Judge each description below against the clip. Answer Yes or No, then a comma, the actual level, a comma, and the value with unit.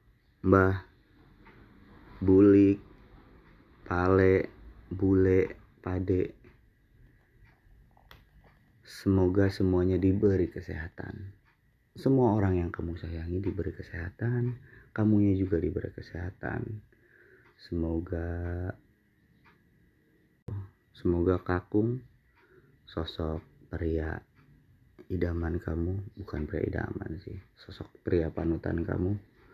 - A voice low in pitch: Yes, very low, 95 Hz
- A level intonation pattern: No, average, 3.6 semitones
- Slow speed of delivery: Yes, slow, 70 wpm